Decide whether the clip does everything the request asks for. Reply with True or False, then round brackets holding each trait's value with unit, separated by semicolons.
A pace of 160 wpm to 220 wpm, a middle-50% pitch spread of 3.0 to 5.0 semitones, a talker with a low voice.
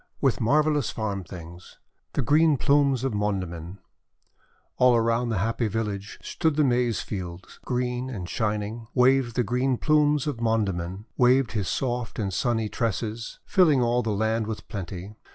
False (150 wpm; 3.8 semitones; 115 Hz)